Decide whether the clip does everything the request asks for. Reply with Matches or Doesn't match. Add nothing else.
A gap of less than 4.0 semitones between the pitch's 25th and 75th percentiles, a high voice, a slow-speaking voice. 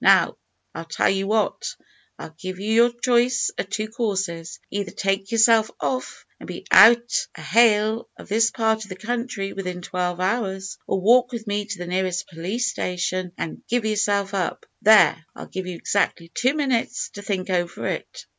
Doesn't match